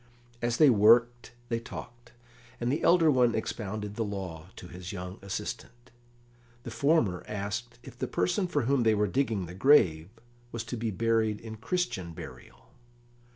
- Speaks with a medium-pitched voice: No, low, 115 Hz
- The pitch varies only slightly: No, average, 3.9 semitones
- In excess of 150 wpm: Yes, average, 160 wpm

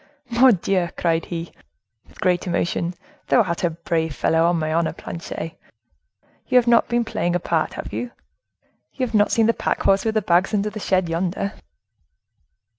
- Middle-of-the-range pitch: Yes, medium, 180 Hz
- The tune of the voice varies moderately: Yes, average, 4.4 semitones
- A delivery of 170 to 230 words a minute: Yes, average, 180 wpm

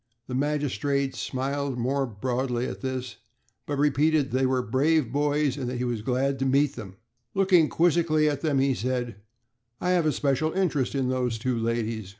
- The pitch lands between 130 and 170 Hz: Yes, low, 135 Hz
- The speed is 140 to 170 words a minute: No, average, 180 wpm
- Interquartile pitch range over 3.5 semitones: No, average, 2.8 semitones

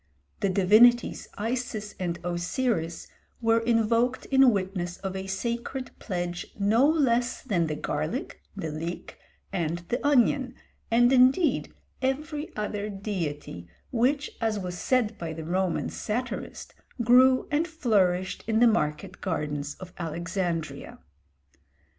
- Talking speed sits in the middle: No, slow, 125 wpm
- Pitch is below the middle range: No, high, 210 Hz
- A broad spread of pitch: Yes, wide, 5.8 semitones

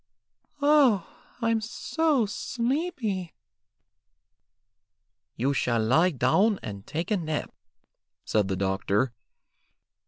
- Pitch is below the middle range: No, medium, 185 Hz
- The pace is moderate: No, slow, 90 wpm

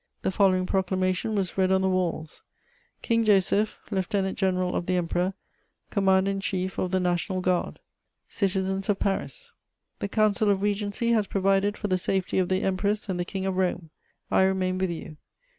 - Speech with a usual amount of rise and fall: No, narrow, 1.5 semitones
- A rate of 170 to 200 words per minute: Yes, average, 175 wpm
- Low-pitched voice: No, high, 190 Hz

